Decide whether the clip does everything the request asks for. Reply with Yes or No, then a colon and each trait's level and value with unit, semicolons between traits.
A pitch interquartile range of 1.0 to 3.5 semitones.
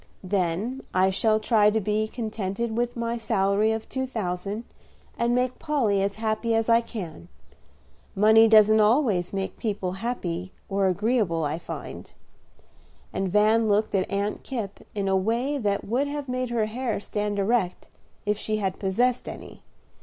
Yes: average, 3.1 semitones